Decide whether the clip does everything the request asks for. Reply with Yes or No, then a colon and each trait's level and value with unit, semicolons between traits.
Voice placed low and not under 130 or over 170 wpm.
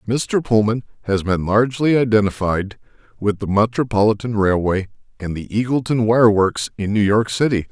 Yes: low, 110 Hz; average, 150 wpm